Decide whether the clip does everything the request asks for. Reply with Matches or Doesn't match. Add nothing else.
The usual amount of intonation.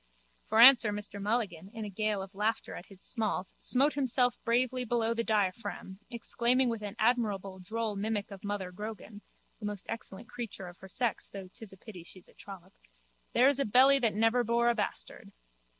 Matches